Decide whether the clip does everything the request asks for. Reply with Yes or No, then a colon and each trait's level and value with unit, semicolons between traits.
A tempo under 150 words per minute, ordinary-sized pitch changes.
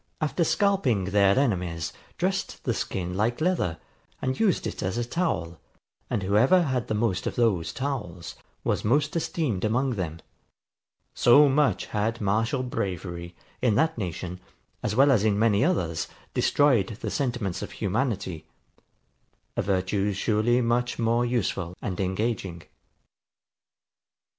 No: average, 140 wpm; wide, 5.7 semitones